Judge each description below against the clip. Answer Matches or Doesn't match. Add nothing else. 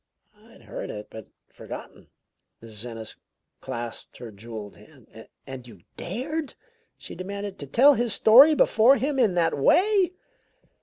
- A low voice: Doesn't match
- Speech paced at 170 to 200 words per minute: Doesn't match